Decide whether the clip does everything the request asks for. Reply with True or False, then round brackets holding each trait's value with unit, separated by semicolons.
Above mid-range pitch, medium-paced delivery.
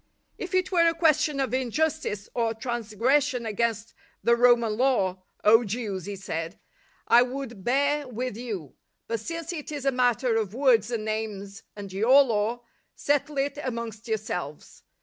True (235 Hz; 170 wpm)